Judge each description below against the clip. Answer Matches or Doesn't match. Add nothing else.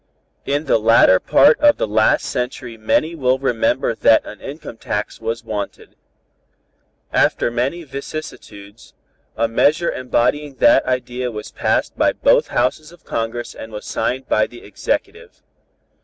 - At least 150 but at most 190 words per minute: Doesn't match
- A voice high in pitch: Doesn't match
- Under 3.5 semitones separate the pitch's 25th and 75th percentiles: Doesn't match